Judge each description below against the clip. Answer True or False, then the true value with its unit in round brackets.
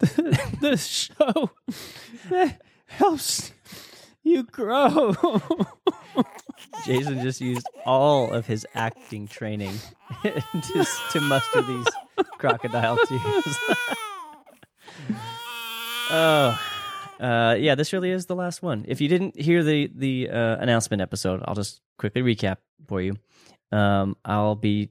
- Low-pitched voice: False (145 Hz)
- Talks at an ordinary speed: False (115 wpm)